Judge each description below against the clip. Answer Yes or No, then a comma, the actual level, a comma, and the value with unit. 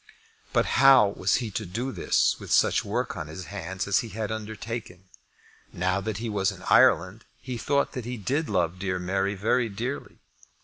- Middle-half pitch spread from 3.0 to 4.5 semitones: Yes, average, 3.9 semitones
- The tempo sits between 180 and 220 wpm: Yes, average, 185 wpm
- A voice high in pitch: No, low, 105 Hz